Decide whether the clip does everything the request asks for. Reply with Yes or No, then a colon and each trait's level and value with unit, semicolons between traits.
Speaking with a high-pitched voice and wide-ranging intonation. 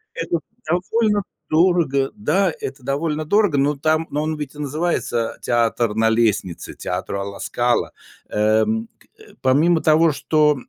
No: medium, 150 Hz; wide, 5.7 semitones